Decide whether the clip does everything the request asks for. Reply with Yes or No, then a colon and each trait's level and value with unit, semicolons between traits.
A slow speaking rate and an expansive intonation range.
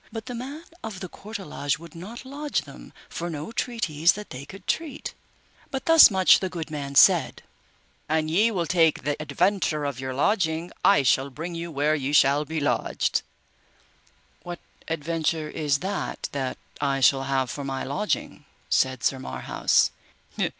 No: average, 165 wpm; wide, 5.7 semitones